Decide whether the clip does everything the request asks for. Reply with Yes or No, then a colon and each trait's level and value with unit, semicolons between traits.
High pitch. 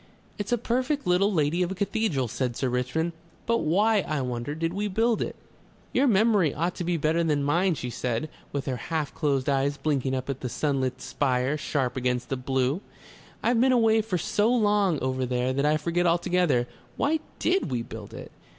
No: medium, 155 Hz